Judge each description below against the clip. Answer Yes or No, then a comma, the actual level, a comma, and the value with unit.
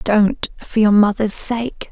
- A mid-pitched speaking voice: No, high, 215 Hz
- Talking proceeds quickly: No, average, 155 wpm